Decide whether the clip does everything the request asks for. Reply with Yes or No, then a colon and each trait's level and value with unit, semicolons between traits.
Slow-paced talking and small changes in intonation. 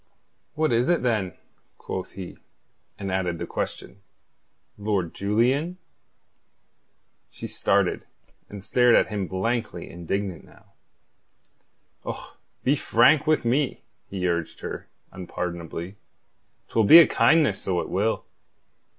No: slow, 115 wpm; average, 5.1 semitones